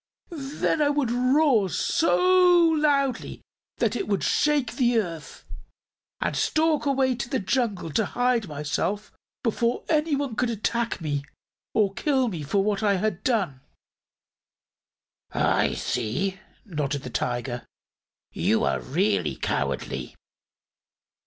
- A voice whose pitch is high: Yes, high, 225 Hz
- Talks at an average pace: No, slow, 120 wpm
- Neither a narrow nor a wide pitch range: No, wide, 8.9 semitones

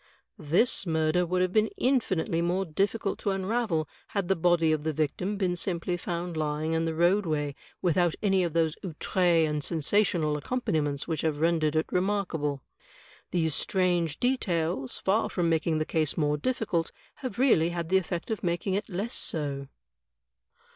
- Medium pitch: Yes, medium, 170 Hz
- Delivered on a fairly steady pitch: No, average, 3.4 semitones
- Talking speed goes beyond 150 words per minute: Yes, average, 165 wpm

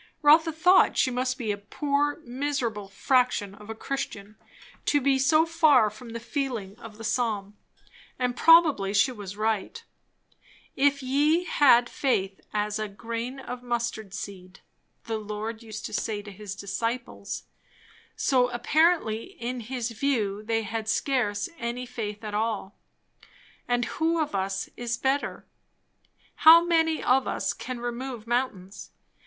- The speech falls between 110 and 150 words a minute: Yes, average, 145 wpm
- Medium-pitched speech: No, high, 235 Hz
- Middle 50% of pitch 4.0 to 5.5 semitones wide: Yes, average, 4.3 semitones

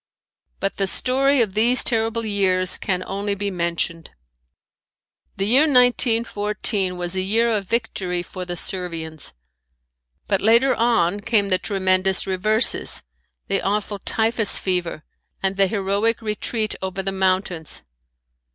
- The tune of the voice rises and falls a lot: No, average, 3.2 semitones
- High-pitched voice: Yes, high, 200 Hz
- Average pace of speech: No, slow, 130 wpm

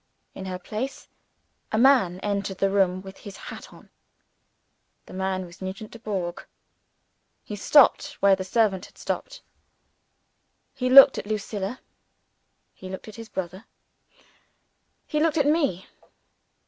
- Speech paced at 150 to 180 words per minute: No, slow, 135 wpm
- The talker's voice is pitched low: No, high, 200 Hz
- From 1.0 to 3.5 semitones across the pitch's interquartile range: No, average, 4.2 semitones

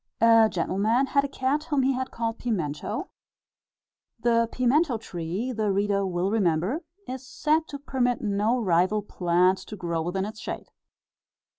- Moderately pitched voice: No, high, 220 Hz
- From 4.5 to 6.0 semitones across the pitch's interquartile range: Yes, wide, 5.4 semitones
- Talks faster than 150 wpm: No, average, 145 wpm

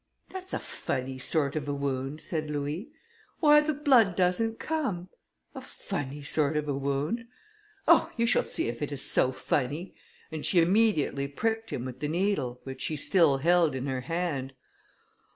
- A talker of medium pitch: Yes, medium, 150 Hz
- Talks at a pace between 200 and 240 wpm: No, average, 170 wpm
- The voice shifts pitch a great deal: Yes, wide, 6.0 semitones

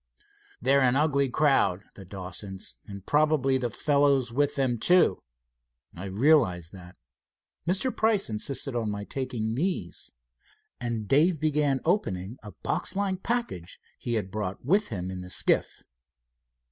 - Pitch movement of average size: No, wide, 7.0 semitones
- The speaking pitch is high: No, low, 130 Hz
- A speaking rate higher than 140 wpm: No, slow, 135 wpm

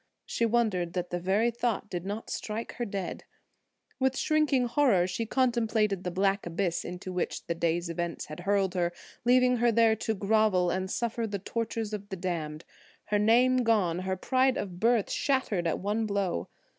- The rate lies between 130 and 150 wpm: No, average, 180 wpm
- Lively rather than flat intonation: No, average, 4.4 semitones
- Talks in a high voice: Yes, high, 205 Hz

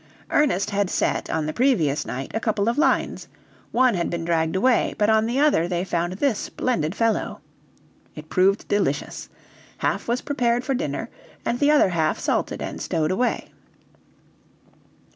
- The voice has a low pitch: No, high, 205 Hz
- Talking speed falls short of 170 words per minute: Yes, average, 160 wpm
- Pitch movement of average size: No, wide, 6.5 semitones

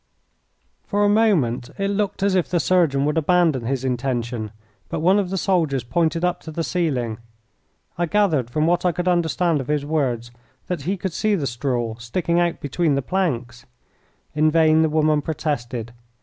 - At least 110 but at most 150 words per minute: No, average, 180 wpm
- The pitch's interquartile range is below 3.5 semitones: No, wide, 5.4 semitones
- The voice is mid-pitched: Yes, medium, 155 Hz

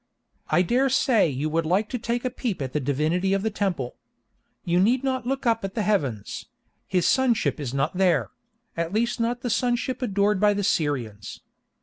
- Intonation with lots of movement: Yes, wide, 6.6 semitones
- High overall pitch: Yes, high, 200 Hz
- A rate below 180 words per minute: No, average, 190 wpm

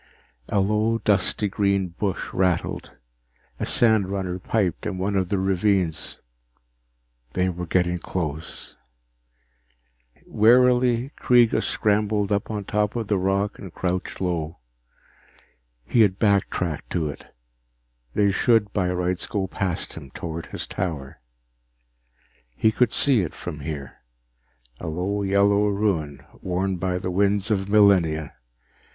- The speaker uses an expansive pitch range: No, narrow, 2.6 semitones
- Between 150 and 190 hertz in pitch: No, very low, 95 Hz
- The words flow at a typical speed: No, slow, 130 wpm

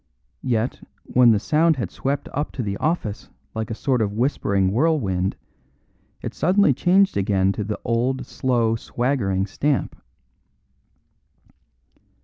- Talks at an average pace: No, slow, 125 wpm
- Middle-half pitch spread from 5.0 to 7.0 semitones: Yes, wide, 5.6 semitones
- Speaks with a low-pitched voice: Yes, low, 120 Hz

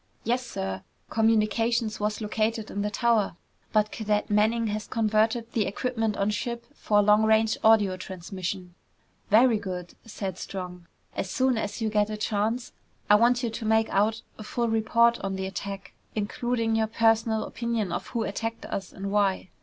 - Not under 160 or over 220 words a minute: Yes, average, 170 wpm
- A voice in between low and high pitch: No, high, 215 Hz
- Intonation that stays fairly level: Yes, narrow, 2.1 semitones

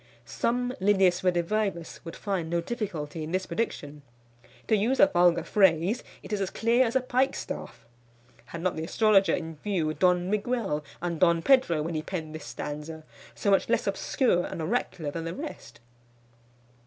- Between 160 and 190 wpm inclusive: Yes, average, 165 wpm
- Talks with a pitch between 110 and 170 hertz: No, medium, 180 Hz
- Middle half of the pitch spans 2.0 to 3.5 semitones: No, average, 4.8 semitones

